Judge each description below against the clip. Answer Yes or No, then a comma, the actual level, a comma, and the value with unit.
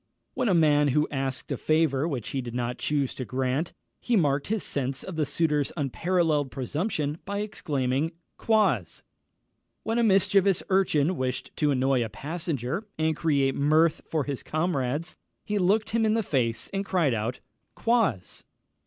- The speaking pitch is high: No, medium, 150 Hz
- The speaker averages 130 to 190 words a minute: Yes, average, 160 wpm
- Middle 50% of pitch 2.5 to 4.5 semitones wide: No, wide, 5.6 semitones